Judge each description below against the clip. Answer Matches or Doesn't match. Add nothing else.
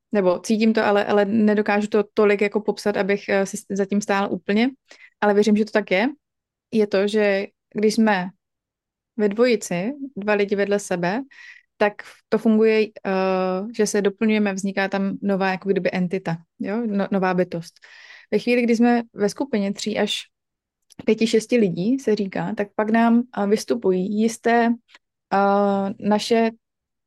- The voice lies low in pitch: Doesn't match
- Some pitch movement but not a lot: Doesn't match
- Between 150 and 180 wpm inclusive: Matches